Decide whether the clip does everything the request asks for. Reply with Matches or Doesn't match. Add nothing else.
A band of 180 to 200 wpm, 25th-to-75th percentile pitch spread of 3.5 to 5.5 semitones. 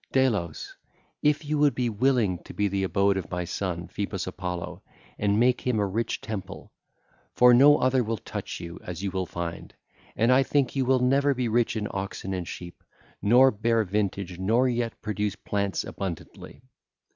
Matches